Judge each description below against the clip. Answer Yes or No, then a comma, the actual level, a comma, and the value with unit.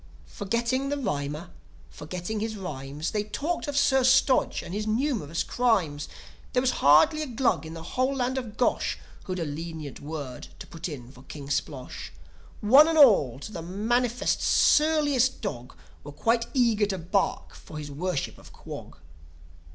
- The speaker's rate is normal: Yes, average, 165 wpm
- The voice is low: No, high, 205 Hz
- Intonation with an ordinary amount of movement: No, wide, 8.7 semitones